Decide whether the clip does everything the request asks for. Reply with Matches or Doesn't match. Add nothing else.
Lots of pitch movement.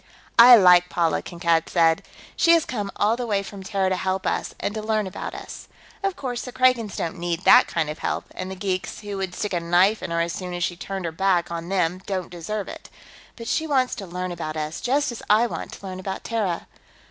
Doesn't match